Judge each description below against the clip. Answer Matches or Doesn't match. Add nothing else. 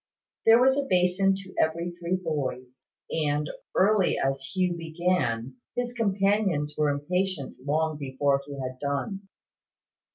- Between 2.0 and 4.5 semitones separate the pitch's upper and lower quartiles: Doesn't match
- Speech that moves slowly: Matches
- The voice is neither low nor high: Matches